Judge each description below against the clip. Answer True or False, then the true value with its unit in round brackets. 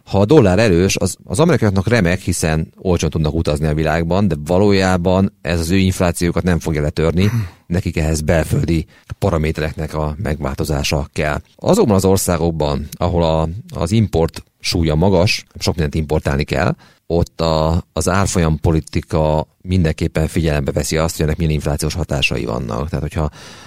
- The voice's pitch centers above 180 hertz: False (85 Hz)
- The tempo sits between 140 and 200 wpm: True (150 wpm)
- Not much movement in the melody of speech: False (3.3 semitones)